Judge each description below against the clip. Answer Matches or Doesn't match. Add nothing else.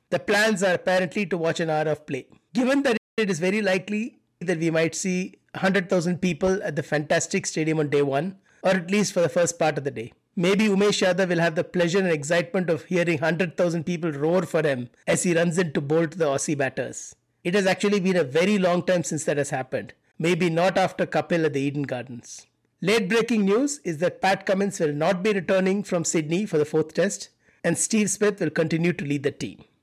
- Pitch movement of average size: Matches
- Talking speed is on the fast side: Matches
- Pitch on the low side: Doesn't match